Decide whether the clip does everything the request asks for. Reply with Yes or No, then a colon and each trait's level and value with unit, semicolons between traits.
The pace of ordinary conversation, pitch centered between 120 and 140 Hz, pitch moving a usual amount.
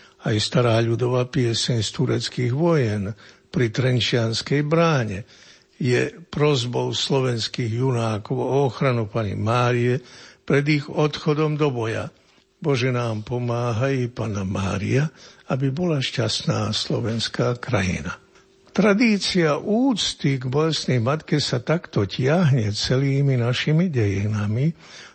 No: slow, 105 wpm; low, 125 Hz; average, 4.8 semitones